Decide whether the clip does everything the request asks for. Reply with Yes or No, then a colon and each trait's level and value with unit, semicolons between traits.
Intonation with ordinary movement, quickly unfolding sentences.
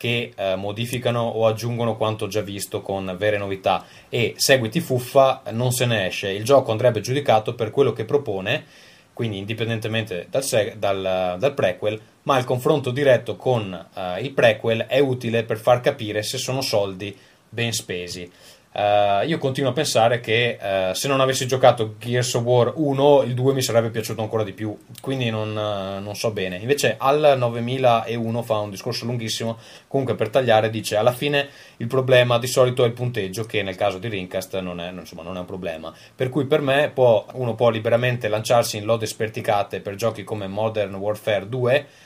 Yes: average, 3.3 semitones; fast, 185 wpm